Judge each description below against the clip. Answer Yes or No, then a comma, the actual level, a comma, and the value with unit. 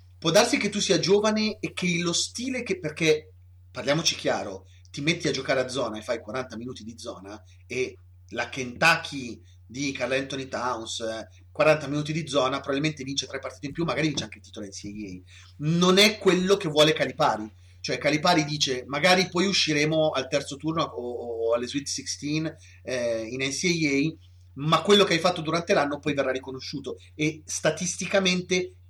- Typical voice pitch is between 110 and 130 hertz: No, medium, 140 Hz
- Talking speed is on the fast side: Yes, fast, 175 wpm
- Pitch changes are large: Yes, wide, 6.7 semitones